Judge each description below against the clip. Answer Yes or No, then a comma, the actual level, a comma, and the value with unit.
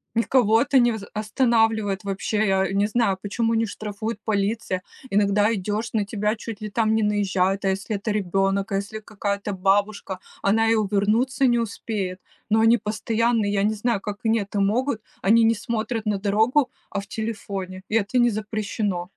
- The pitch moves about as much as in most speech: No, narrow, 2.1 semitones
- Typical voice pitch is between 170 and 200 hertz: No, high, 210 Hz